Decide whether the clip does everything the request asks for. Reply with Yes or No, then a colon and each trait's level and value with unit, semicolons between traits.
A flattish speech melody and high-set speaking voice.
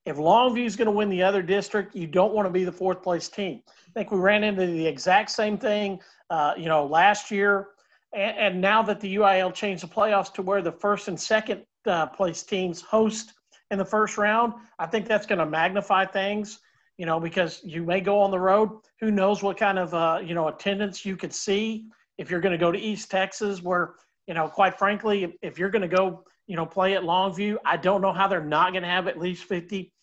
Yes: narrow, 2.3 semitones; high, 195 Hz